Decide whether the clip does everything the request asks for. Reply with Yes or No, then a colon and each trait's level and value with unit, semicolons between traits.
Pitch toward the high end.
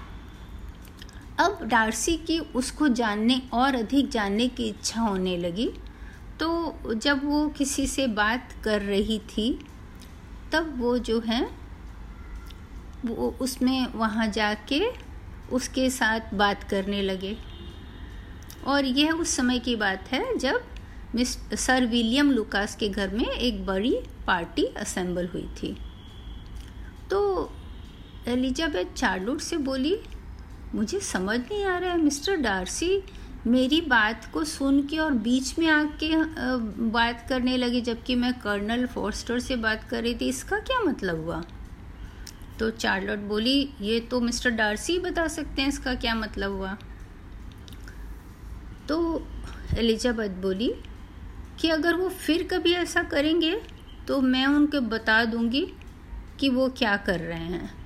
Yes: high, 245 Hz